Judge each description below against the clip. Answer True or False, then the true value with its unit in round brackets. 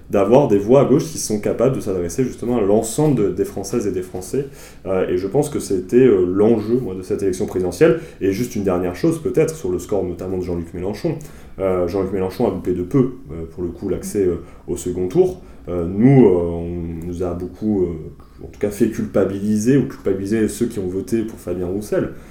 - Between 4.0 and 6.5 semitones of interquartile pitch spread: True (5.4 semitones)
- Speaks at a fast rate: True (225 wpm)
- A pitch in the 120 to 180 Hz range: False (95 Hz)